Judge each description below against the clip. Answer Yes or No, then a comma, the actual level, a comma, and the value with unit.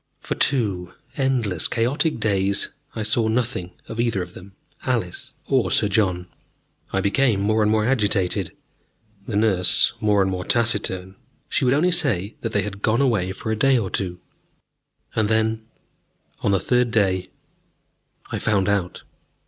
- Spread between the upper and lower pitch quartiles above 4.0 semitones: No, average, 3.6 semitones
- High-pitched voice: No, low, 105 Hz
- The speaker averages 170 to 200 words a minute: No, average, 155 wpm